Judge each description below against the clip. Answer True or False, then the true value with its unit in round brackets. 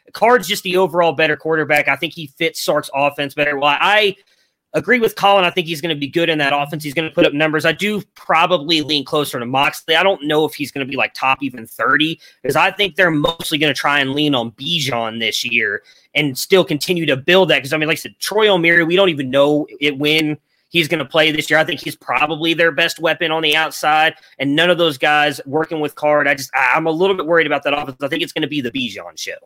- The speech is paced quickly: True (265 wpm)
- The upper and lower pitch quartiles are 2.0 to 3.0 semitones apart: True (2.6 semitones)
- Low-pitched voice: False (155 Hz)